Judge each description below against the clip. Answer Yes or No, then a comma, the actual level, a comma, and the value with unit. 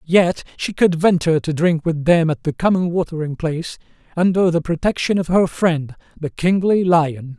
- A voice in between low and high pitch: Yes, medium, 170 Hz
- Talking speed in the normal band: Yes, average, 180 wpm